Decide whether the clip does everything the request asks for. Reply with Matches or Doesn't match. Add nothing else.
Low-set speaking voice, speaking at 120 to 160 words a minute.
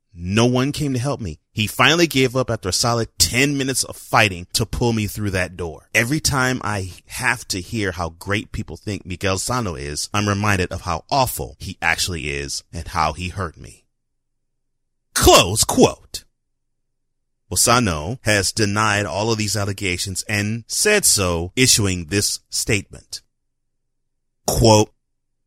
Matches